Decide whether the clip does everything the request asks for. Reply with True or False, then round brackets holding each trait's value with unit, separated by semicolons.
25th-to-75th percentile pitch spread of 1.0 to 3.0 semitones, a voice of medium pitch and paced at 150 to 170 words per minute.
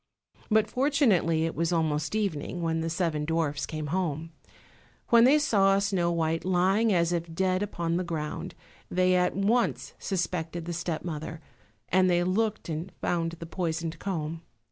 True (2.7 semitones; 175 Hz; 160 wpm)